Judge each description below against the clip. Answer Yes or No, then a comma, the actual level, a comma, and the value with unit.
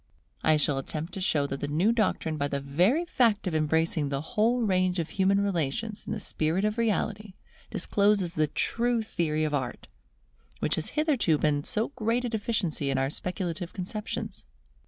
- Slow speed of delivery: No, average, 175 wpm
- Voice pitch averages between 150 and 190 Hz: Yes, medium, 185 Hz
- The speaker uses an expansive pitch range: Yes, wide, 5.8 semitones